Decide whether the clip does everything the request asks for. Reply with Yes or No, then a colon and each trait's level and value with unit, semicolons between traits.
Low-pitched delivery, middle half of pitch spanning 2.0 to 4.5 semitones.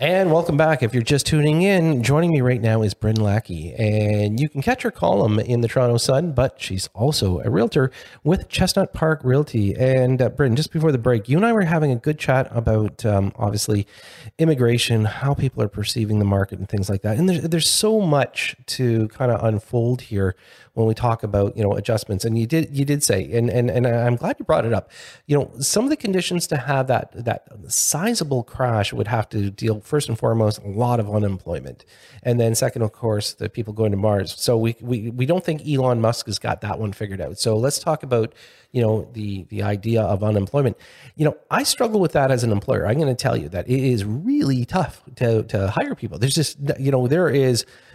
No: low, 120 Hz; average, 4.9 semitones